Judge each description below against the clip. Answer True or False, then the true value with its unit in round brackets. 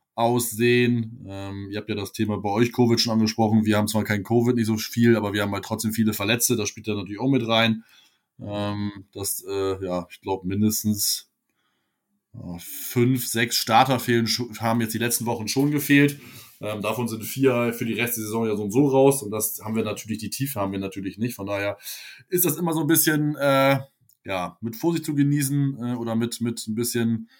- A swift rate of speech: True (215 wpm)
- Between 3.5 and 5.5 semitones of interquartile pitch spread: False (2.8 semitones)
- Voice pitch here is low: True (115 Hz)